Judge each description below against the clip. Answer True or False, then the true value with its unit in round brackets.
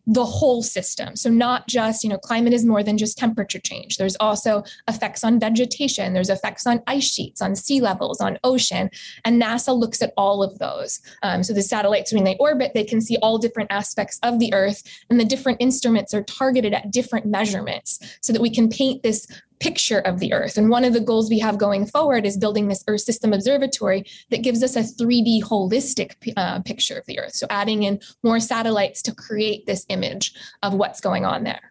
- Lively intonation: False (3.1 semitones)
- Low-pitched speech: False (225 Hz)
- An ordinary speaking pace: False (210 wpm)